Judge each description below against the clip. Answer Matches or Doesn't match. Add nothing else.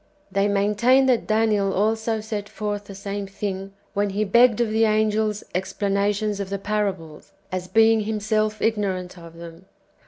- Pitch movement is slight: Matches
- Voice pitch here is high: Matches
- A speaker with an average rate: Matches